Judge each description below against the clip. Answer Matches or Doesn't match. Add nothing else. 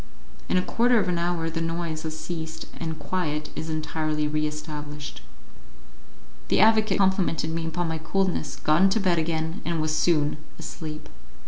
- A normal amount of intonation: Doesn't match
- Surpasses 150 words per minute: Matches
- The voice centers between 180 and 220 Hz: Doesn't match